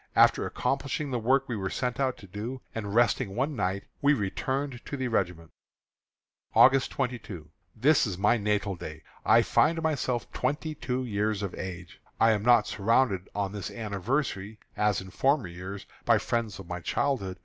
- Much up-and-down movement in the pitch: No, average, 5.0 semitones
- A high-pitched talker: No, low, 110 Hz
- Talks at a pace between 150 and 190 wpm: Yes, average, 175 wpm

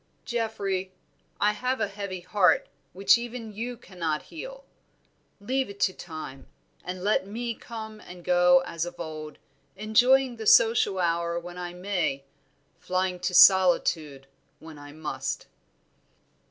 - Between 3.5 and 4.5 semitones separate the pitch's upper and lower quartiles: Yes, average, 4.1 semitones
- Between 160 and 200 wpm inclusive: No, slow, 135 wpm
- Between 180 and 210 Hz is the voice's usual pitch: Yes, medium, 185 Hz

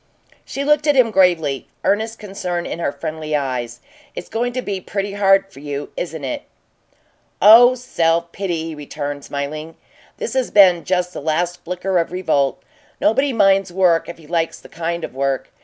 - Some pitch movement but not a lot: Yes, average, 4.5 semitones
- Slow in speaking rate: No, average, 175 wpm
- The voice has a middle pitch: Yes, medium, 175 Hz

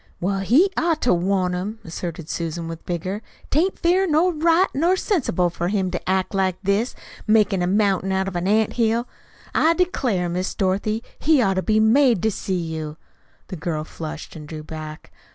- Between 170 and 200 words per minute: Yes, average, 190 wpm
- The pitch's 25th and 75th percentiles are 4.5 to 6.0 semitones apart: Yes, wide, 5.4 semitones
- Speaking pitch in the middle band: No, high, 195 Hz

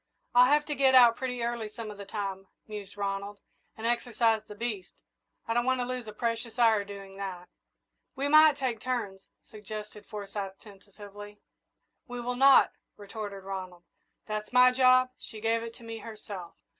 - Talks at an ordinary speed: Yes, average, 175 wpm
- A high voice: Yes, high, 220 Hz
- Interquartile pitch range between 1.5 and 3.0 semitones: No, average, 3.4 semitones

